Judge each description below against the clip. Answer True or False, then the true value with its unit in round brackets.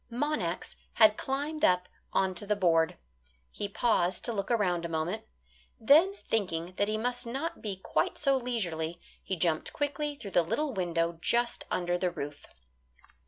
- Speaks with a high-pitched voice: True (205 Hz)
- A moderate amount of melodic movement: False (6.1 semitones)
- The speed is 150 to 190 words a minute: True (160 wpm)